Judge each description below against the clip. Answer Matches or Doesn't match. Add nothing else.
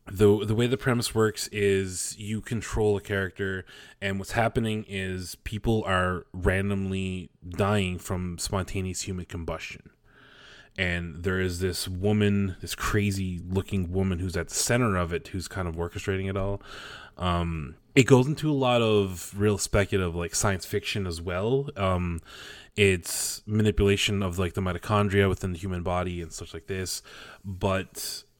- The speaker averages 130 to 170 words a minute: Matches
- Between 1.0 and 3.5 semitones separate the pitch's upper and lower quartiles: Matches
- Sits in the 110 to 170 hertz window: Doesn't match